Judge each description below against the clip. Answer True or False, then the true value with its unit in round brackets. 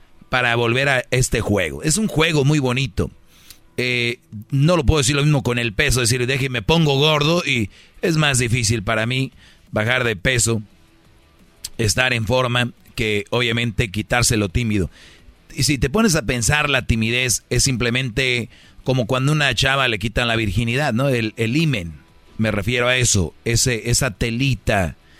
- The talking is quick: False (170 wpm)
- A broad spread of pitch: False (3.2 semitones)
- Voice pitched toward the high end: False (120 Hz)